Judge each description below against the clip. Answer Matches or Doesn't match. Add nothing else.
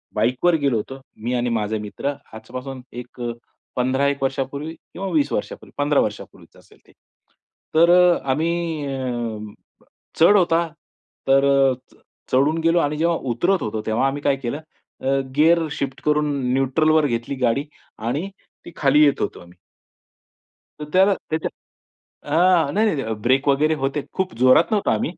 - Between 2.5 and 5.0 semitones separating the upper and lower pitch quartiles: Matches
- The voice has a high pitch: Doesn't match